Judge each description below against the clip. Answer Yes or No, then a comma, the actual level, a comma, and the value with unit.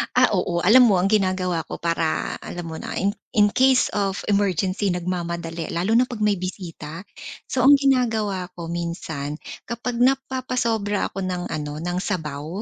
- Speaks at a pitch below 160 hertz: No, medium, 185 Hz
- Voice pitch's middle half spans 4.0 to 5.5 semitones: Yes, average, 4.5 semitones